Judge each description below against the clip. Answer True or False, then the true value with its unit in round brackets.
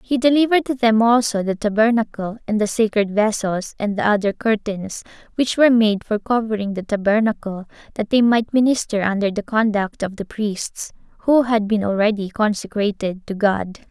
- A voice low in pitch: False (215 Hz)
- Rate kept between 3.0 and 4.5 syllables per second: False (5.2 syllables/s)